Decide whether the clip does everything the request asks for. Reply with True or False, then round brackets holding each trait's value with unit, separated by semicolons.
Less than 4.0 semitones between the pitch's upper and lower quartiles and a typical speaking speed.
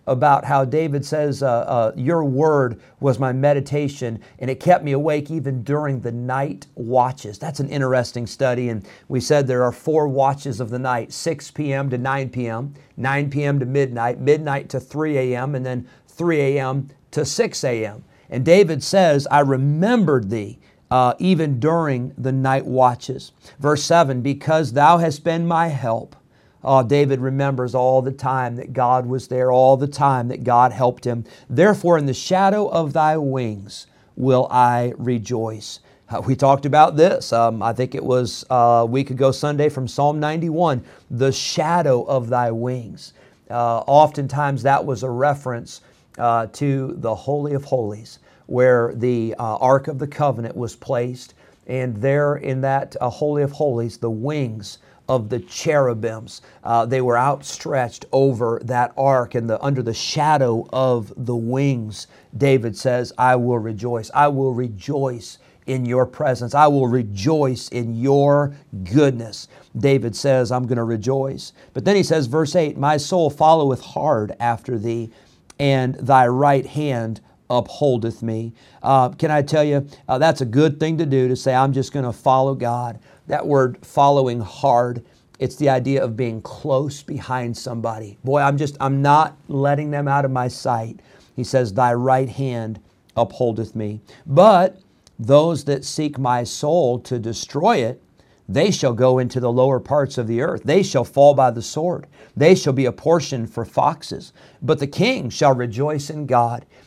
True (2.8 semitones; 170 wpm)